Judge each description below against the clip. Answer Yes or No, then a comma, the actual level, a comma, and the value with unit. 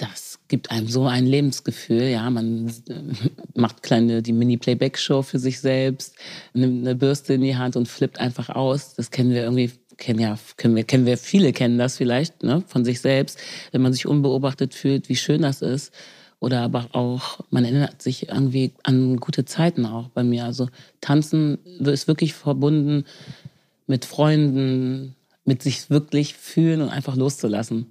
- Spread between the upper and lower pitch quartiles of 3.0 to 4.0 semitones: No, narrow, 2.4 semitones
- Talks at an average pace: Yes, average, 170 wpm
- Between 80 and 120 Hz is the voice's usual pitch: No, low, 130 Hz